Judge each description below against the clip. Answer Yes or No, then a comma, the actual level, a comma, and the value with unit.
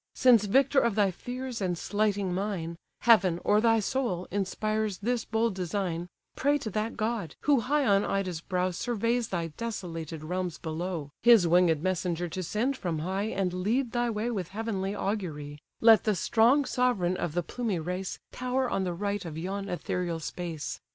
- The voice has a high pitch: Yes, high, 195 Hz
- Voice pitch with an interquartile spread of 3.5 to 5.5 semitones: Yes, average, 4.5 semitones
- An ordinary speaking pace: Yes, average, 170 wpm